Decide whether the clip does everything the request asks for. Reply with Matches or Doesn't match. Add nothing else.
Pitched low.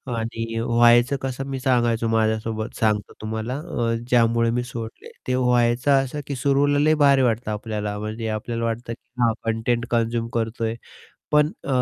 Matches